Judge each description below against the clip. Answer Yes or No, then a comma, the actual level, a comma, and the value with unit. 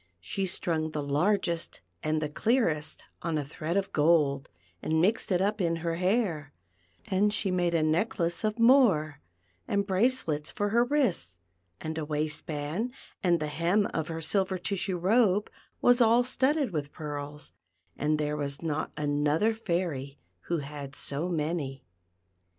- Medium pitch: Yes, medium, 165 Hz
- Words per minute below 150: No, average, 155 wpm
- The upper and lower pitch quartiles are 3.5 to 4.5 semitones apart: No, average, 5.0 semitones